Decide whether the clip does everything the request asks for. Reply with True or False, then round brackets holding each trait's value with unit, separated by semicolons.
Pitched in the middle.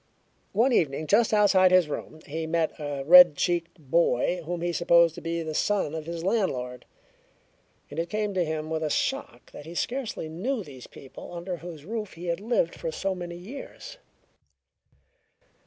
True (170 Hz)